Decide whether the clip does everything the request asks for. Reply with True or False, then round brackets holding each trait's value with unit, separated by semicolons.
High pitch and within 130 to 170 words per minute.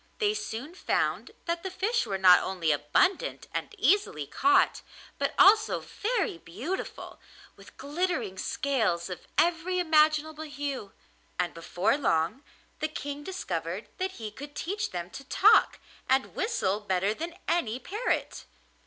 True (290 Hz; 135 wpm)